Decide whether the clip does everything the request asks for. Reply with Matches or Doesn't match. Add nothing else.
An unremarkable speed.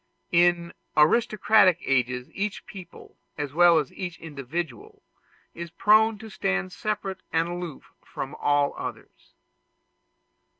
Doesn't match